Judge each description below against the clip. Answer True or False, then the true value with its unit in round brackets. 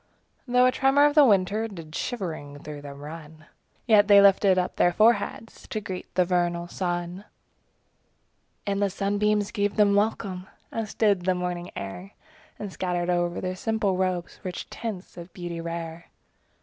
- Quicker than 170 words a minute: False (160 wpm)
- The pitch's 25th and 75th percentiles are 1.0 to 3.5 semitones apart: True (3.1 semitones)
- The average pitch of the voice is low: False (185 Hz)